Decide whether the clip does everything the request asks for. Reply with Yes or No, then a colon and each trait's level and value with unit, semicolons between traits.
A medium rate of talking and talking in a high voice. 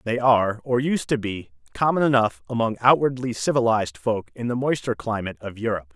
No: average, 180 wpm; low, 120 Hz